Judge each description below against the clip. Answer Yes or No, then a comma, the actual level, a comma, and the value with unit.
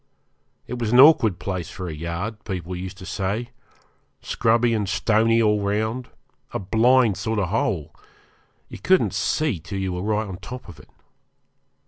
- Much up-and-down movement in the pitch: No, average, 3.7 semitones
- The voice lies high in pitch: No, low, 105 Hz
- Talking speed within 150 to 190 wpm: Yes, average, 170 wpm